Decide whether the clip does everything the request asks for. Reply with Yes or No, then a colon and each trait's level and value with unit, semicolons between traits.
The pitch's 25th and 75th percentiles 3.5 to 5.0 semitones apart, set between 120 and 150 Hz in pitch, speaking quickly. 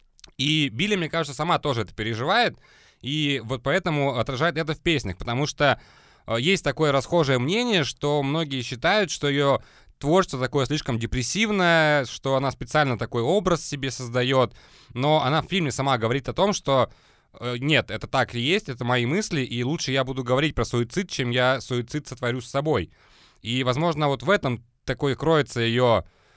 Yes: average, 3.9 semitones; low, 135 Hz; fast, 170 wpm